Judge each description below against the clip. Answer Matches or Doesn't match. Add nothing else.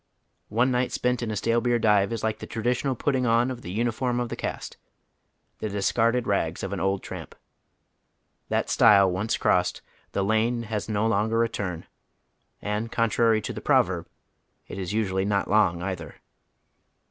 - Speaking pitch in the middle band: Doesn't match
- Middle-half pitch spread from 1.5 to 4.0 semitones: Matches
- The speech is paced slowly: Doesn't match